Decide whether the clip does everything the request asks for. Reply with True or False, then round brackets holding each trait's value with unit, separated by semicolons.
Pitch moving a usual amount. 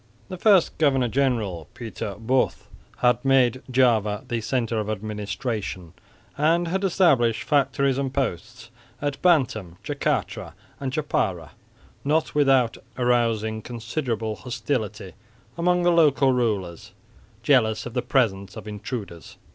True (4.4 semitones)